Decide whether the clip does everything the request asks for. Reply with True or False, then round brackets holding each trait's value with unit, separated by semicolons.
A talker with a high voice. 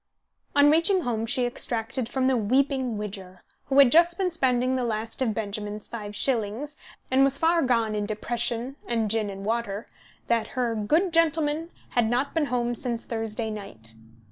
True (240 Hz)